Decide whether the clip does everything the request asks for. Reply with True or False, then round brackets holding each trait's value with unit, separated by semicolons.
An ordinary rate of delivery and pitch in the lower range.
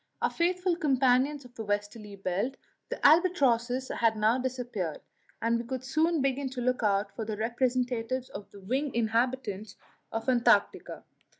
False (160 wpm; 245 Hz)